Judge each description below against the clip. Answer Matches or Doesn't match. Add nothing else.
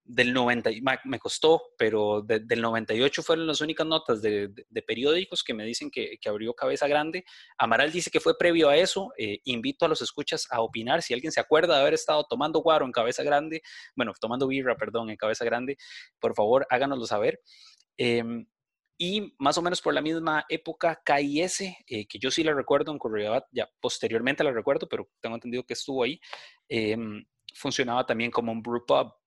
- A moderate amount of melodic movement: Doesn't match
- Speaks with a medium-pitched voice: Matches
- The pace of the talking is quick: Matches